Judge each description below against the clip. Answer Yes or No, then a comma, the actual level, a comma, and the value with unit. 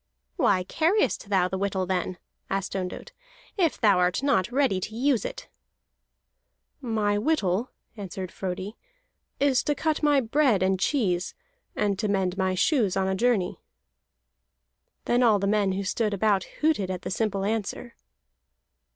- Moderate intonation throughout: Yes, average, 4.7 semitones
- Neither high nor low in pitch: No, high, 205 Hz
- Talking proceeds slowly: No, average, 150 wpm